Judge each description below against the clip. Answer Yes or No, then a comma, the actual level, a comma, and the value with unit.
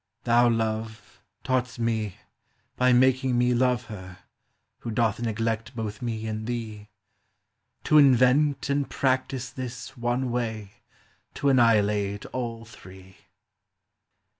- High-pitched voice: No, low, 120 Hz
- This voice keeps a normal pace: No, slow, 115 wpm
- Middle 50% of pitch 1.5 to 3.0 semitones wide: Yes, narrow, 2.5 semitones